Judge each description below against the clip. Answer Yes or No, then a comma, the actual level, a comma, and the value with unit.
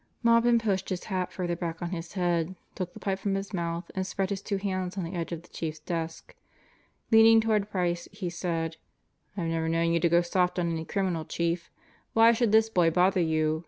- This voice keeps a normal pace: No, fast, 215 wpm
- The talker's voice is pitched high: No, medium, 180 Hz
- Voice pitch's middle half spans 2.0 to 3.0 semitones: Yes, narrow, 2.6 semitones